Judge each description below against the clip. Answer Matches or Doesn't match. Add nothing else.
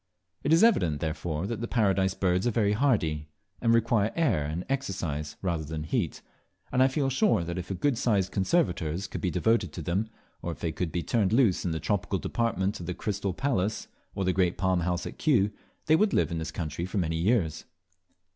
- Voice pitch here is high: Doesn't match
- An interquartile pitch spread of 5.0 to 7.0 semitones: Matches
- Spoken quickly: Matches